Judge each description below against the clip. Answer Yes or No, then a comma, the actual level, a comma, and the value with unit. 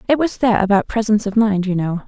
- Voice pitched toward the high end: Yes, high, 210 Hz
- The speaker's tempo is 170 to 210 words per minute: No, fast, 260 wpm